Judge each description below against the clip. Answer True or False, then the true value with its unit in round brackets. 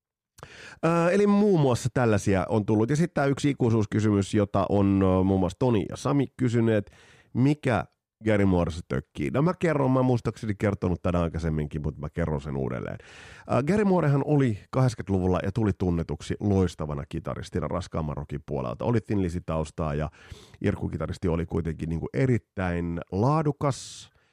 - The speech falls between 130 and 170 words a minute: True (145 wpm)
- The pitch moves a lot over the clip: True (6.9 semitones)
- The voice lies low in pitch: True (100 Hz)